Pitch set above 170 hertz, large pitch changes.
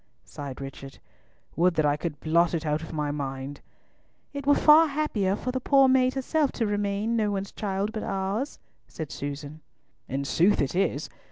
Yes: high, 190 Hz; wide, 7.8 semitones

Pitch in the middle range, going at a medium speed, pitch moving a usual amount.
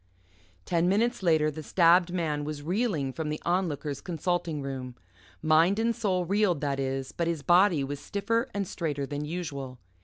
Yes: medium, 165 Hz; average, 165 wpm; average, 4.2 semitones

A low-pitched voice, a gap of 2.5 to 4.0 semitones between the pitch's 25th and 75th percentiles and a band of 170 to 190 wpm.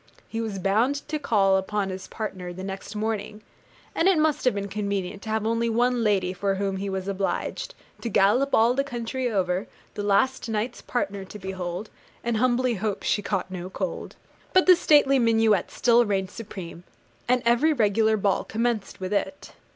No: high, 210 Hz; average, 3.6 semitones; average, 180 wpm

